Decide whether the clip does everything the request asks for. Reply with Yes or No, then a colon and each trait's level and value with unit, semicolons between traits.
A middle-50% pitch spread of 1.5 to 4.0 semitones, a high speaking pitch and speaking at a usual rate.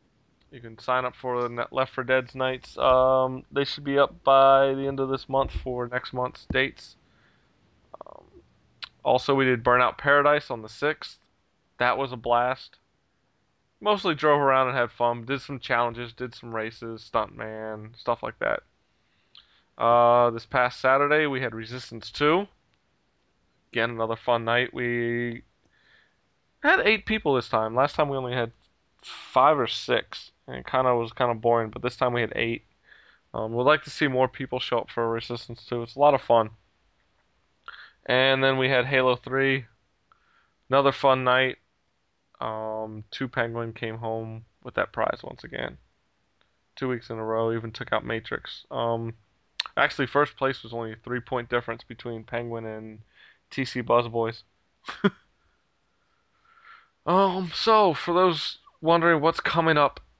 No: average, 2.8 semitones; low, 125 Hz; average, 160 wpm